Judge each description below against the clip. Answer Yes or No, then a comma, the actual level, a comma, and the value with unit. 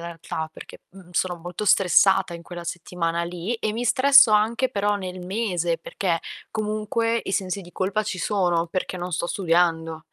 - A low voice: No, medium, 185 Hz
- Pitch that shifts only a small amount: No, average, 3.5 semitones